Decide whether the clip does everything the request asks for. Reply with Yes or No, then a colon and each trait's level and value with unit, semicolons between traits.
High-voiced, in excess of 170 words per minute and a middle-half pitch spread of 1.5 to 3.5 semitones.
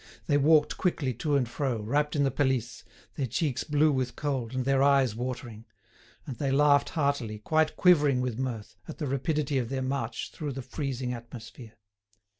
No: low, 135 Hz; average, 180 wpm; average, 3.0 semitones